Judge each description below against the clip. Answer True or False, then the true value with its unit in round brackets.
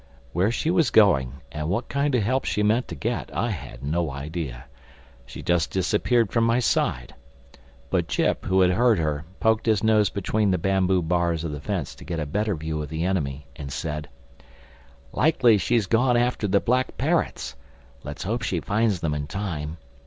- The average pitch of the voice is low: True (95 Hz)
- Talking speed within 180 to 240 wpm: True (190 wpm)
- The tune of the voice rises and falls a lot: True (6.4 semitones)